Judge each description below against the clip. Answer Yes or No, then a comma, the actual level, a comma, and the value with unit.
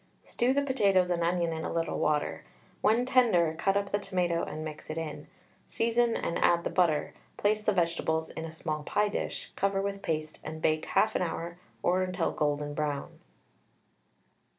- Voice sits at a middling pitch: Yes, medium, 175 Hz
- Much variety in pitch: No, average, 4.1 semitones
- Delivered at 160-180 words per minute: Yes, average, 175 wpm